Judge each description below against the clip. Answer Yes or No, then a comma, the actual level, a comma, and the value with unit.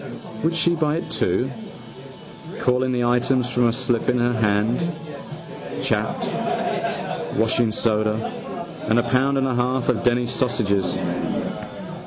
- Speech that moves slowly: Yes, slow, 125 wpm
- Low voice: Yes, low, 120 Hz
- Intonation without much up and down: Yes, narrow, 2.3 semitones